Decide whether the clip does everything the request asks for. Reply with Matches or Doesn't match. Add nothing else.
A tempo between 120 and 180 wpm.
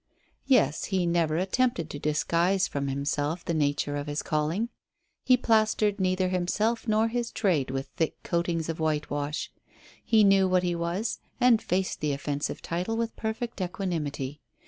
Matches